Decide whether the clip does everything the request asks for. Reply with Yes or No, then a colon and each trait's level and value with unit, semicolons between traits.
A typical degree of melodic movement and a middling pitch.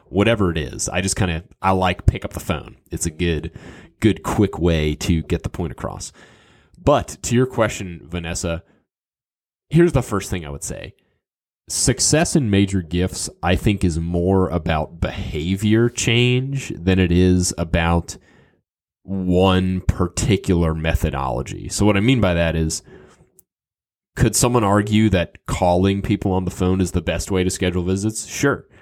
No: average, 3.2 semitones; very low, 95 Hz